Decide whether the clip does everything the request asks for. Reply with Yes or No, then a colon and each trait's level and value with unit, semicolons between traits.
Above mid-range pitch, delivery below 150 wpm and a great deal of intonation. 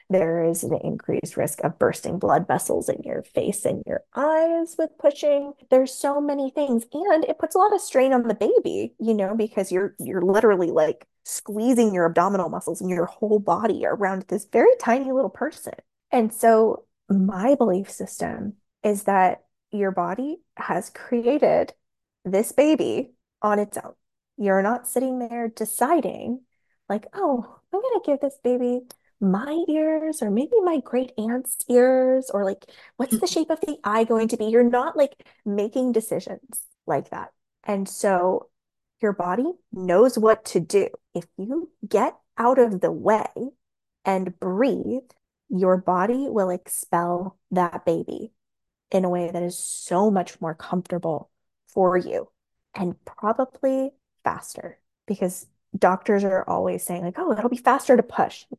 No: high, 230 Hz; average, 160 wpm; wide, 6.0 semitones